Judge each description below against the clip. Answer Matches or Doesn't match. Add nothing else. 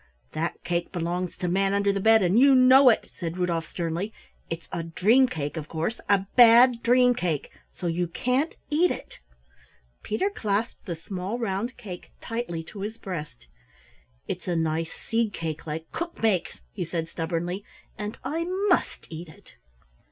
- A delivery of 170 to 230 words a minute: Doesn't match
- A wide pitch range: Matches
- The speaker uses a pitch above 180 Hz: Matches